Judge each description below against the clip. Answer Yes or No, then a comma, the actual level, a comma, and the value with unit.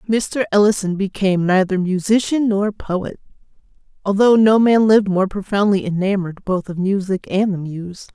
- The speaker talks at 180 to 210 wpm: No, average, 145 wpm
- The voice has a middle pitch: No, high, 195 Hz